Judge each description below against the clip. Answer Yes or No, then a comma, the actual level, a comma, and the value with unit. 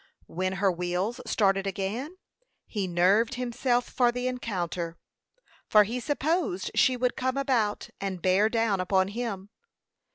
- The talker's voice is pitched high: Yes, high, 210 Hz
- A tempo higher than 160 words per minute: No, slow, 135 wpm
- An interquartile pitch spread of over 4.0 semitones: Yes, average, 4.8 semitones